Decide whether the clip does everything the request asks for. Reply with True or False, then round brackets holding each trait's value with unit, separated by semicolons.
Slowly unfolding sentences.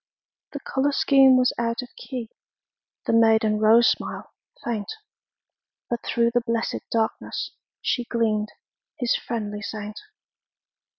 True (120 wpm)